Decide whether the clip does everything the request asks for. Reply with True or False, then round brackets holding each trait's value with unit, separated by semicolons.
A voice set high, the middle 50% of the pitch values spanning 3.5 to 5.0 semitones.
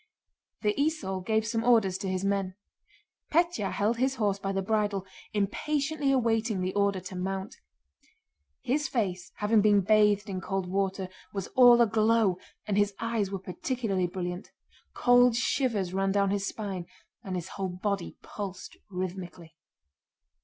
False (200 Hz; 3.1 semitones)